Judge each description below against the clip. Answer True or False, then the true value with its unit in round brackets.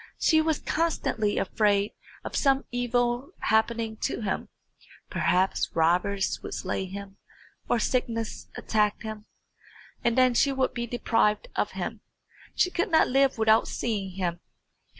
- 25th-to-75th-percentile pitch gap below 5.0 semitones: True (3.8 semitones)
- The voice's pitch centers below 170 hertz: False (225 Hz)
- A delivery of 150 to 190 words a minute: False (135 wpm)